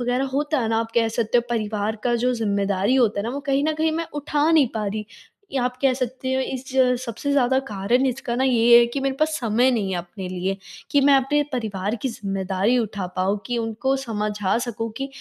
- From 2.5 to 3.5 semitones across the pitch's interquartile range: No, average, 4.0 semitones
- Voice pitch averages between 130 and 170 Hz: No, high, 240 Hz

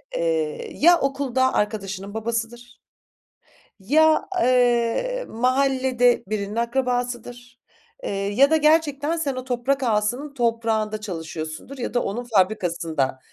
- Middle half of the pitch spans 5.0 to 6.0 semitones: No, average, 4.1 semitones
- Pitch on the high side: Yes, high, 240 Hz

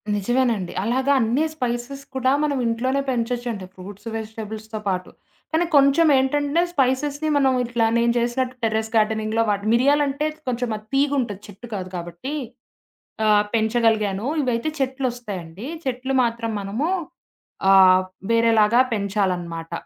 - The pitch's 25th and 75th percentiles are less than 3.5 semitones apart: No, average, 3.8 semitones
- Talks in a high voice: Yes, high, 235 Hz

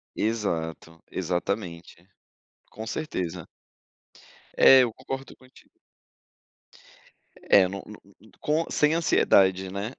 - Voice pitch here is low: Yes, low, 100 Hz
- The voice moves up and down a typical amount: No, wide, 6.1 semitones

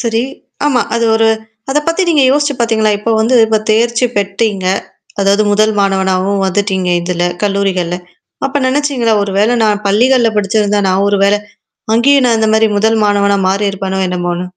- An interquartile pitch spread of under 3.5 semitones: Yes, average, 2.9 semitones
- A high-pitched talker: Yes, high, 210 Hz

